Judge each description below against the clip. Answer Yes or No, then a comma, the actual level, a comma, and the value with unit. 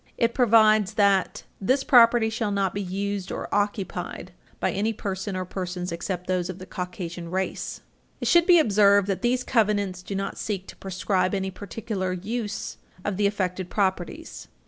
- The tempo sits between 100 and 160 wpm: No, average, 170 wpm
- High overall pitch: Yes, high, 200 Hz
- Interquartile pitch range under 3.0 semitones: Yes, narrow, 2.6 semitones